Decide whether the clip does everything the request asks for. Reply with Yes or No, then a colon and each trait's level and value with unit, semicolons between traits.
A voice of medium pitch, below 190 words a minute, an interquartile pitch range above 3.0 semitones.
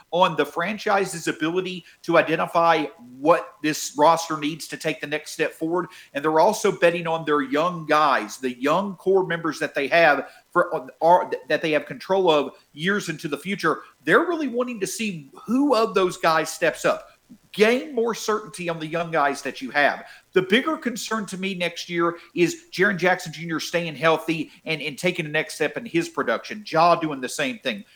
No: medium, 170 Hz; average, 195 wpm; average, 4.2 semitones